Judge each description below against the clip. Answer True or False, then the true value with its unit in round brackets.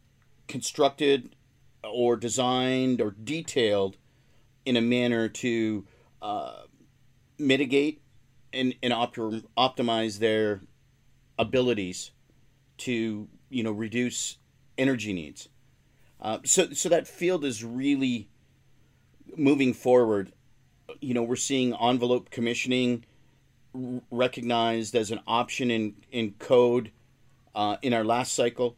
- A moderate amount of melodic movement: False (2.0 semitones)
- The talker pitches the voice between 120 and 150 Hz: True (125 Hz)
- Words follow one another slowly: True (105 wpm)